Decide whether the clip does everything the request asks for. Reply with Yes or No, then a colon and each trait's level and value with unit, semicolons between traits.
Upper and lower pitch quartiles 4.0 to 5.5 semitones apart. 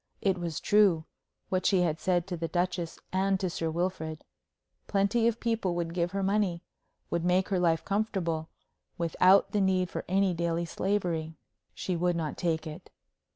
No: narrow, 2.5 semitones